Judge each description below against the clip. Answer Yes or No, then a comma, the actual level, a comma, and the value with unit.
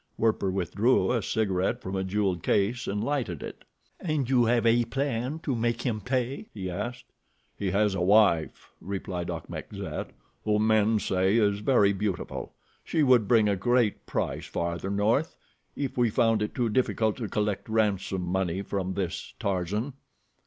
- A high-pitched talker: No, low, 105 Hz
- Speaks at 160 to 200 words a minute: Yes, average, 165 wpm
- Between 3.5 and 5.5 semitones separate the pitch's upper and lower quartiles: Yes, average, 3.9 semitones